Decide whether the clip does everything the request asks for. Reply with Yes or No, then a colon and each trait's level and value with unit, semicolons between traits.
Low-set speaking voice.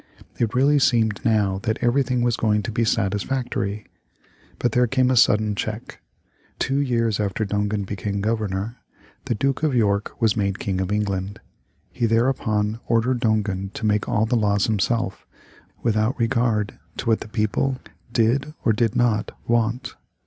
Yes: low, 110 Hz